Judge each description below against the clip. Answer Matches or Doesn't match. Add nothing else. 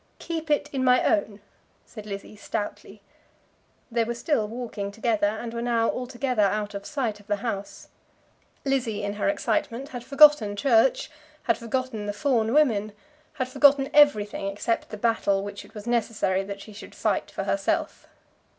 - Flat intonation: Doesn't match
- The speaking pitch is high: Matches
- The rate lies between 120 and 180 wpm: Matches